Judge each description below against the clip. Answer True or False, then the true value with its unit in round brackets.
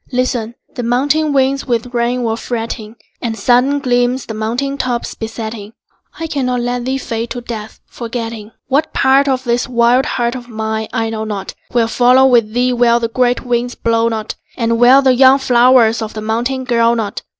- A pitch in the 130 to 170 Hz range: False (240 Hz)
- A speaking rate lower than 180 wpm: False (185 wpm)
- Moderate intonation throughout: False (2.0 semitones)